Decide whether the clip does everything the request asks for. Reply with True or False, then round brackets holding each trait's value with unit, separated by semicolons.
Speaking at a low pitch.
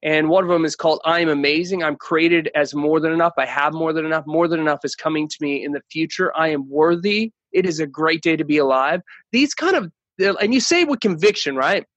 False (160 Hz)